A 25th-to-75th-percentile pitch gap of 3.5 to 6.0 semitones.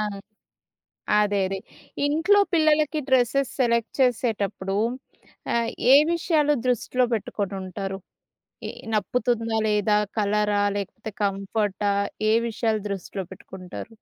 Yes: average, 3.9 semitones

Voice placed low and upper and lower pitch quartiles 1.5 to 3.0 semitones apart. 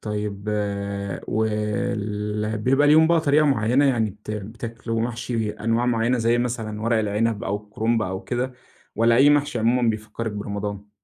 Yes: low, 115 Hz; narrow, 2.5 semitones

